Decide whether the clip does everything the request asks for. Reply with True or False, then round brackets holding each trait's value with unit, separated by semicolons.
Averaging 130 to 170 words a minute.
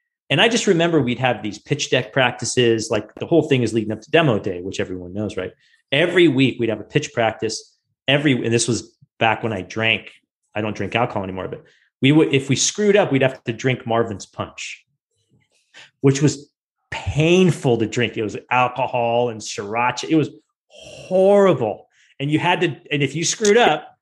False (195 wpm)